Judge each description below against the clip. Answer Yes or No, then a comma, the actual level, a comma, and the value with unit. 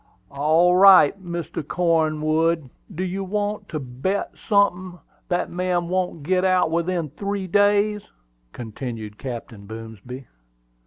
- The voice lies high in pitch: No, medium, 175 Hz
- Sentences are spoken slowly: Yes, slow, 115 wpm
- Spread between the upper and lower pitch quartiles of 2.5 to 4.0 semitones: No, average, 4.7 semitones